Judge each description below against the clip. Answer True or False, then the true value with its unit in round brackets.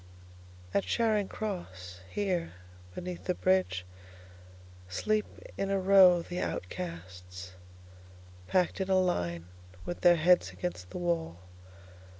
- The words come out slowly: True (105 wpm)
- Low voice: True (95 Hz)